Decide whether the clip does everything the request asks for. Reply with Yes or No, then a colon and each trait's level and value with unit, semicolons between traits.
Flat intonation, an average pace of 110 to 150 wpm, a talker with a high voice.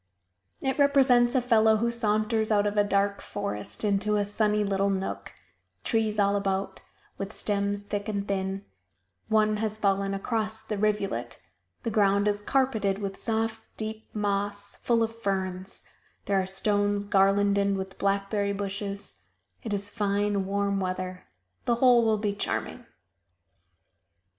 Yes: narrow, 1.6 semitones; average, 145 wpm; high, 205 Hz